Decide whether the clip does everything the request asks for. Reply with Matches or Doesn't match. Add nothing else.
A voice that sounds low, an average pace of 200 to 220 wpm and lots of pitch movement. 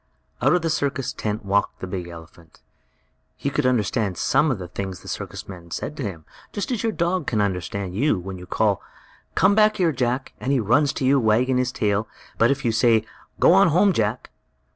Matches